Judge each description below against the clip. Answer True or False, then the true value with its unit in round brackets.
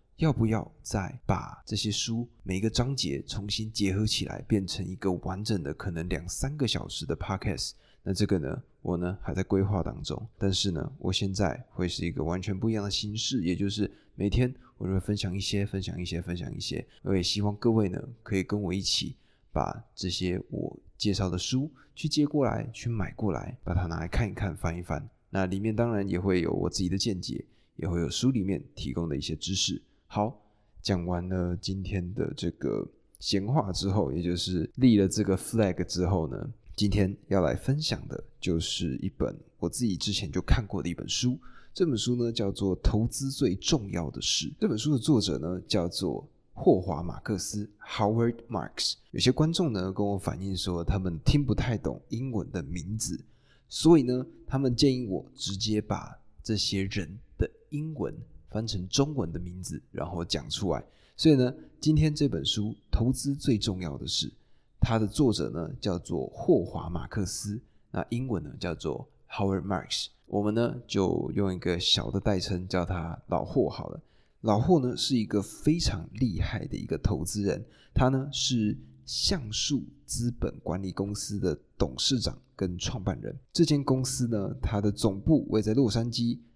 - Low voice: True (100 Hz)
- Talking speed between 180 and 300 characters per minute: True (280 characters per minute)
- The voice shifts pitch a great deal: False (4.6 semitones)